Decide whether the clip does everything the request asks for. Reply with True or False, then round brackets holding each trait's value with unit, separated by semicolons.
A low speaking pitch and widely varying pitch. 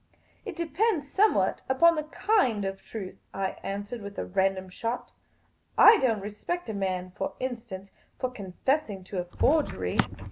False (215 Hz; 7.4 semitones)